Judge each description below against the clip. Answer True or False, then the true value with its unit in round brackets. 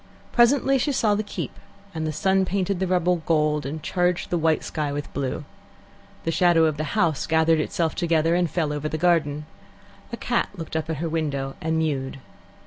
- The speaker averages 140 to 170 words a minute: False (195 wpm)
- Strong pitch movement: False (2.7 semitones)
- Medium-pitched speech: True (160 Hz)